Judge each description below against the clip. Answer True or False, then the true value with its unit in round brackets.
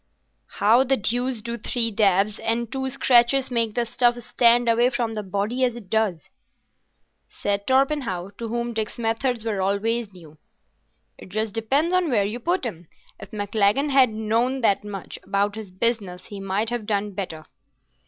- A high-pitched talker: True (225 Hz)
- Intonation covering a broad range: False (3.2 semitones)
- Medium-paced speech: True (170 wpm)